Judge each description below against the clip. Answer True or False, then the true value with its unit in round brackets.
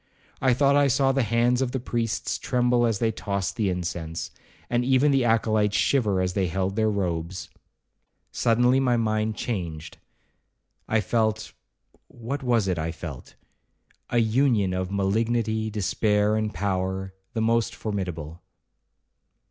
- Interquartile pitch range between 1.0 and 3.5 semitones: False (4.0 semitones)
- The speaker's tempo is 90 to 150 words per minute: True (135 wpm)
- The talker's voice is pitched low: True (110 Hz)